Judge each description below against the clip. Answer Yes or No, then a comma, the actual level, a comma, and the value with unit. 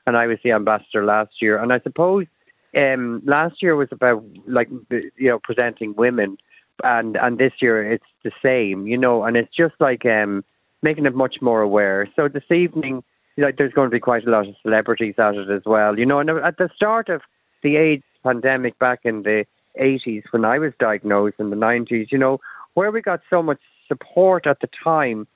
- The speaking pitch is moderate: No, low, 120 Hz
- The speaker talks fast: Yes, fast, 215 wpm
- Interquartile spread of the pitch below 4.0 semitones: No, average, 4.7 semitones